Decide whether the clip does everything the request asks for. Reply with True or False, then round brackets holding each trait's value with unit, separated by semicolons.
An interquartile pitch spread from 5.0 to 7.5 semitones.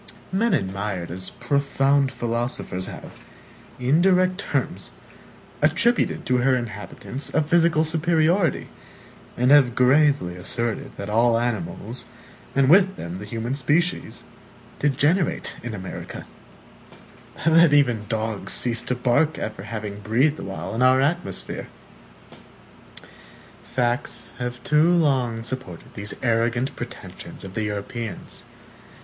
True (5.5 semitones)